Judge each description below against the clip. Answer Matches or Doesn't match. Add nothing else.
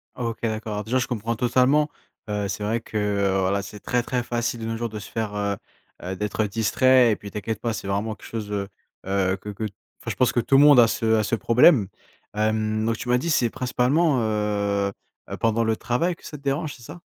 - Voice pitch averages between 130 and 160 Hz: Doesn't match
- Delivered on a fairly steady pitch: Doesn't match